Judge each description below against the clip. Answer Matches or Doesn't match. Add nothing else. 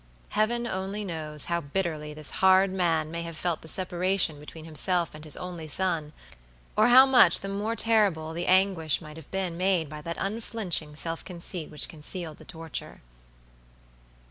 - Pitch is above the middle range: Doesn't match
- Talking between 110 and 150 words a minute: Doesn't match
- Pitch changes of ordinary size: Matches